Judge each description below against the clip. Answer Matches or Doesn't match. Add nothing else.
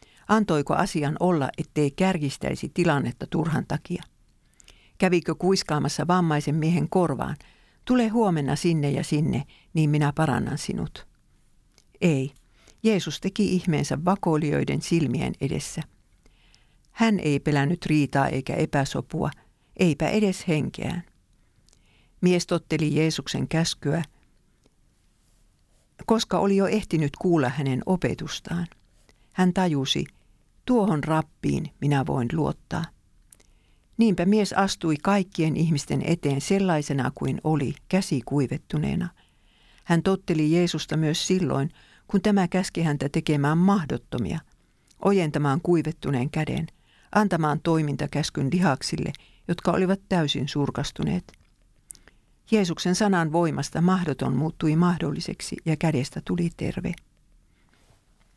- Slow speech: Matches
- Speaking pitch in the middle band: Matches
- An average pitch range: Matches